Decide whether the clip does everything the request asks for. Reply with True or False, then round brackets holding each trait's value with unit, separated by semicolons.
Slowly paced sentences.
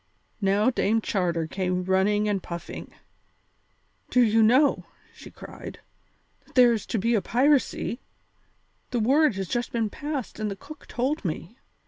False (150 wpm)